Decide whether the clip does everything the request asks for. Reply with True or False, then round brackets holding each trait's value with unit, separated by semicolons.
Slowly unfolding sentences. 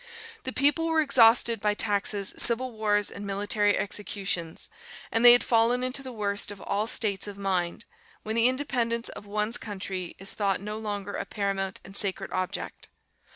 False (170 wpm)